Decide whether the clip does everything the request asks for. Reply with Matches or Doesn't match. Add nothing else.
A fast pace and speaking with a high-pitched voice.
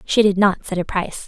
Matches